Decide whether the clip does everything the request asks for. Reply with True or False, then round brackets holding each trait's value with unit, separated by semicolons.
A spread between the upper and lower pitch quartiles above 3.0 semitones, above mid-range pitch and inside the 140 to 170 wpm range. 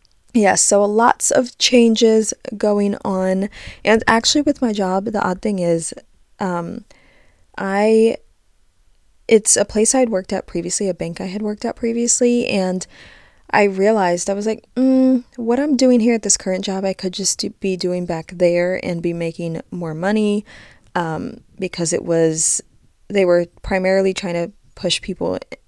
True (3.7 semitones; 200 Hz; 165 wpm)